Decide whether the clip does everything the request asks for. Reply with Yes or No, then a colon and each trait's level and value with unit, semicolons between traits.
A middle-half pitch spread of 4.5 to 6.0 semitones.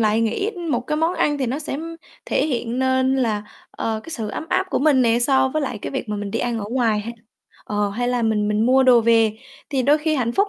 No: average, 3.4 semitones